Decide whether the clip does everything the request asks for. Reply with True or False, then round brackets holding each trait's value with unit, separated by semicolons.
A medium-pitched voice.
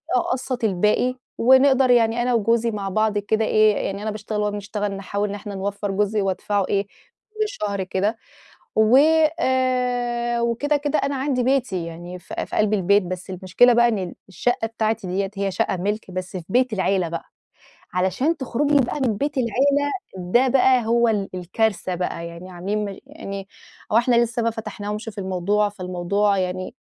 False (215 Hz)